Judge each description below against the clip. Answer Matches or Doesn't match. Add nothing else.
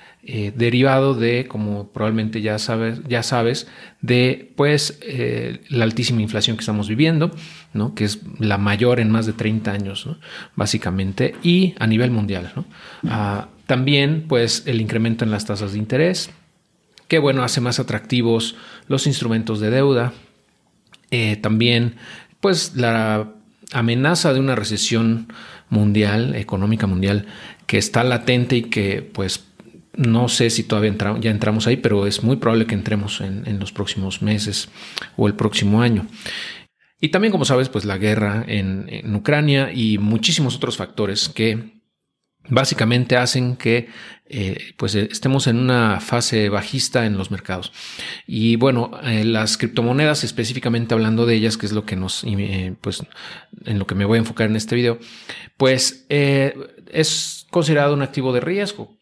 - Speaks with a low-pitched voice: Matches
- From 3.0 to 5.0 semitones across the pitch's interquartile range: Matches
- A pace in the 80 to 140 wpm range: Doesn't match